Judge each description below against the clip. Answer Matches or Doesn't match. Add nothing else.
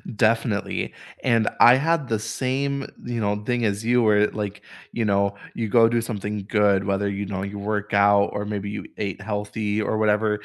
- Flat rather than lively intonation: Matches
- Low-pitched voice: Matches